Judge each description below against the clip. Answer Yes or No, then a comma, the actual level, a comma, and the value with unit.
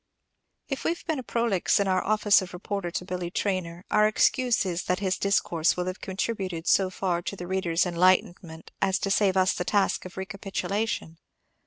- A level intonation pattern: Yes, narrow, 2.2 semitones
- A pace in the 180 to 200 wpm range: Yes, average, 185 wpm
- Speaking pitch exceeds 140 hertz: Yes, high, 190 Hz